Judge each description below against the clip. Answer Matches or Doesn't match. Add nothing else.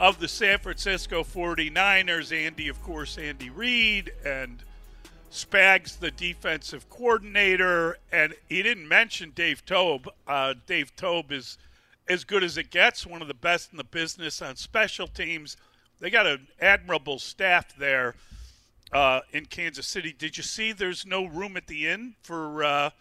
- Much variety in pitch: Doesn't match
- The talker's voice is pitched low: Doesn't match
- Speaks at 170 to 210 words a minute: Doesn't match